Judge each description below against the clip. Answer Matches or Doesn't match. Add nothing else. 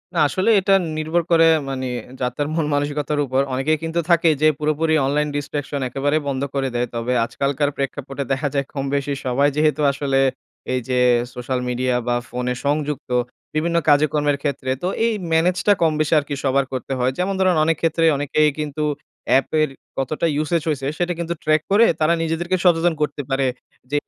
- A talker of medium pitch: Matches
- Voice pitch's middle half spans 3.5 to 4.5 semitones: Doesn't match